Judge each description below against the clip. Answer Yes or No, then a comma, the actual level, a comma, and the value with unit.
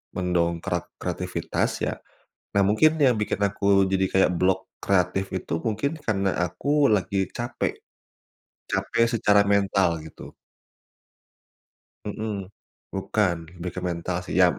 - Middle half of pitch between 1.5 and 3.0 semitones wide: Yes, average, 2.7 semitones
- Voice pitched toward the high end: No, very low, 95 Hz